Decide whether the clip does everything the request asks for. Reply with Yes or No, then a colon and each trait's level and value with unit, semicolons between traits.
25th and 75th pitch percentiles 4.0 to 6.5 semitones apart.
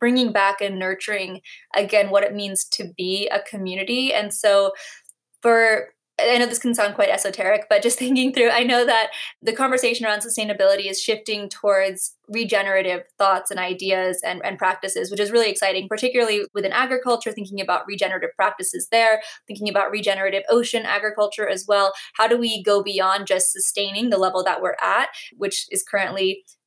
No: average, 3.2 semitones